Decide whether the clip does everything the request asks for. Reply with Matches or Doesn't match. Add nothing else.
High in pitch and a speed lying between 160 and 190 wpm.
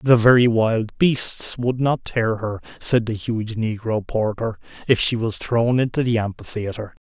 Doesn't match